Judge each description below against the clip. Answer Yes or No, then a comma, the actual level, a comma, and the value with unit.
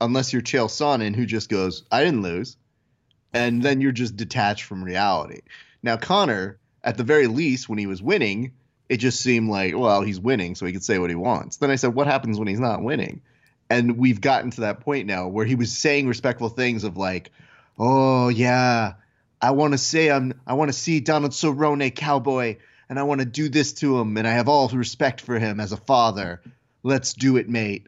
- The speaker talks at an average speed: No, fast, 215 wpm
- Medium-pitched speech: No, low, 125 Hz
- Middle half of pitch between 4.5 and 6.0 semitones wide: No, average, 3.6 semitones